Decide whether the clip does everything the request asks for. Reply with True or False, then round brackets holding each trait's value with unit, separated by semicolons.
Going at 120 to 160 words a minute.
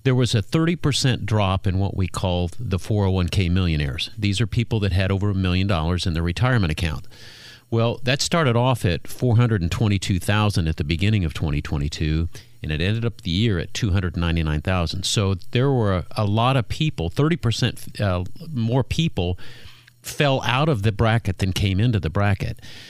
False (170 wpm)